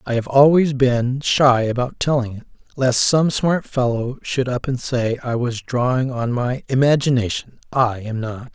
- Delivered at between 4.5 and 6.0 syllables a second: No, 4.3 syllables/s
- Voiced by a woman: No, male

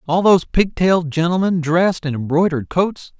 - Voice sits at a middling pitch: Yes, medium, 170 Hz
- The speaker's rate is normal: Yes, average, 150 wpm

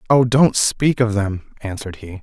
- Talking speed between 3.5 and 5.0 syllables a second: Yes, 4.8 syllables/s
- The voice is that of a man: Yes, male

